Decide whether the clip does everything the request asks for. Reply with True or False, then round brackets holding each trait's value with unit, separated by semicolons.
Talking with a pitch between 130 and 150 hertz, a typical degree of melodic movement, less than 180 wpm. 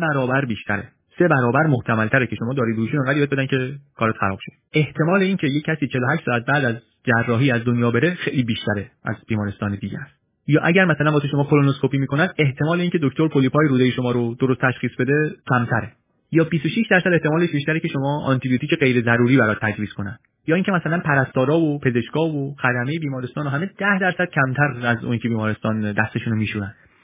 False (135 Hz; 4.4 semitones; 185 wpm)